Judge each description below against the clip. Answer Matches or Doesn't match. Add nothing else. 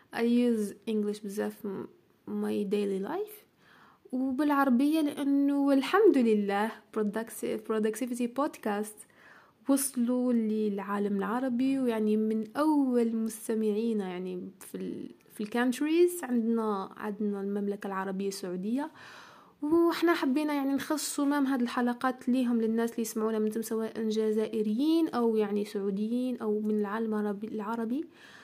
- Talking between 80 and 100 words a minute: Doesn't match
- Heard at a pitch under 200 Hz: Doesn't match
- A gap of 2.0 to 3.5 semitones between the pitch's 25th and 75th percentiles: Doesn't match